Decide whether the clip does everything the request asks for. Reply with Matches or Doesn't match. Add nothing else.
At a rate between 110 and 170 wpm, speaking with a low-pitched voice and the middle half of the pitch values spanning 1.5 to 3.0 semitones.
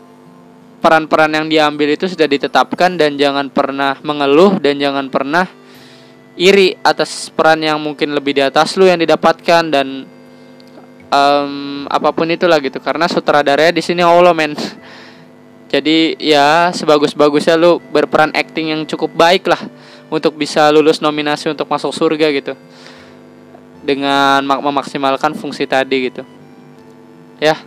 Doesn't match